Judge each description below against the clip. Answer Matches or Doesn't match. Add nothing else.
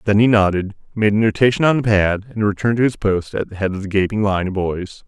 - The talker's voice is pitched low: Matches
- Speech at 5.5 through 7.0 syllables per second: Matches